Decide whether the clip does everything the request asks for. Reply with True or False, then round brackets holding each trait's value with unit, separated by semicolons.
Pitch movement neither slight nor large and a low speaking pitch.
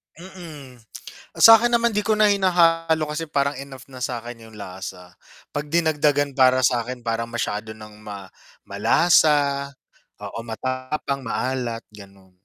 False (5.7 semitones; 130 Hz)